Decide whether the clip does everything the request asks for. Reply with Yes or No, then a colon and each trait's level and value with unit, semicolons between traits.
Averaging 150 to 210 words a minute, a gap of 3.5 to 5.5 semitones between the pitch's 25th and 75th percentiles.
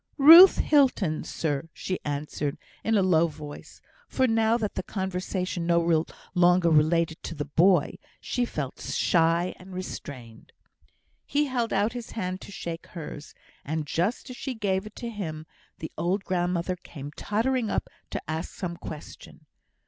Yes: average, 155 wpm; average, 4.9 semitones